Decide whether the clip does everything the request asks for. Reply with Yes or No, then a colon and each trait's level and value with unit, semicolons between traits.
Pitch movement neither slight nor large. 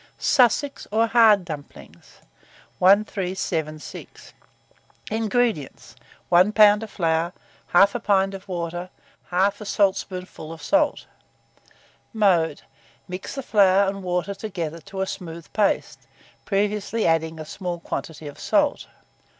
Yes: average, 3.7 semitones